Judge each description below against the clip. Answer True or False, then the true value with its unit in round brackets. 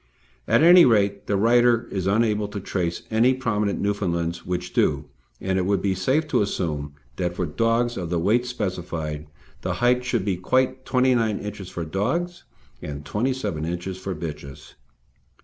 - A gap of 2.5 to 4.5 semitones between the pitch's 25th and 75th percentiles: False (5.4 semitones)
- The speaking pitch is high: False (100 Hz)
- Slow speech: False (165 wpm)